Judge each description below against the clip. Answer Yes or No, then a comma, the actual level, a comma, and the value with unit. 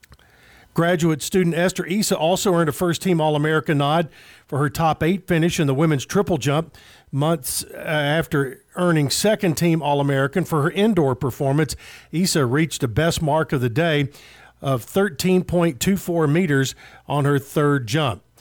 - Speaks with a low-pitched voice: No, medium, 155 Hz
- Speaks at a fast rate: No, average, 155 wpm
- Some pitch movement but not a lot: Yes, average, 3.5 semitones